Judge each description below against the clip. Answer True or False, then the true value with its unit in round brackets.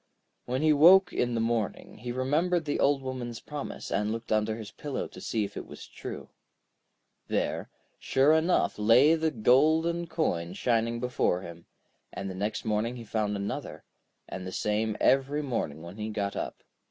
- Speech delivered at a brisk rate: False (175 wpm)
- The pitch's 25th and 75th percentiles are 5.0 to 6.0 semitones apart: True (5.5 semitones)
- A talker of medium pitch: False (120 Hz)